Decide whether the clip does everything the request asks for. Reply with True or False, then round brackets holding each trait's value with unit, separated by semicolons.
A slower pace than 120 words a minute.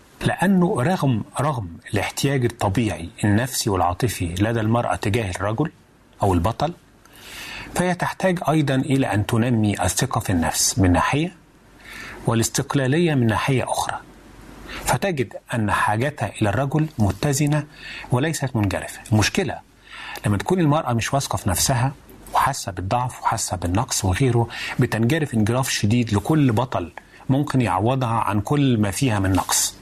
False (125 wpm)